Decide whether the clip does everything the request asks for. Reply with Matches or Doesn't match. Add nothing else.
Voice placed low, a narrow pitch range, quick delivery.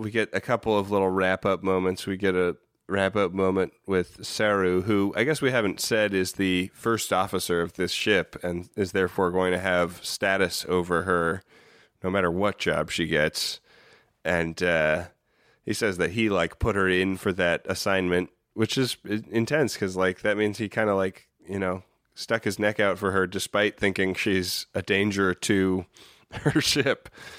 Doesn't match